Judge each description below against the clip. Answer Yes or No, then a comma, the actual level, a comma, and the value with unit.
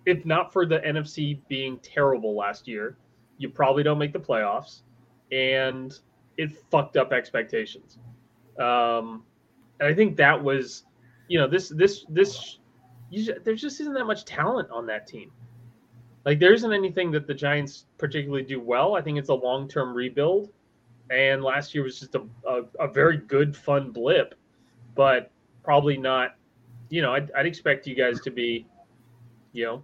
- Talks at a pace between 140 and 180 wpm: Yes, average, 170 wpm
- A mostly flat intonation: No, average, 3.8 semitones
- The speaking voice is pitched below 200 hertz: Yes, low, 135 Hz